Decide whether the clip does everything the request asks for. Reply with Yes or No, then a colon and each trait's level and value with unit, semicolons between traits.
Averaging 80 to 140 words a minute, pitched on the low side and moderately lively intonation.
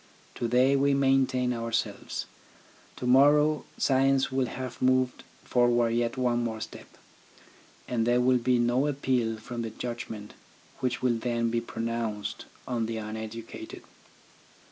No: slow, 135 wpm; low, 120 Hz; narrow, 1.9 semitones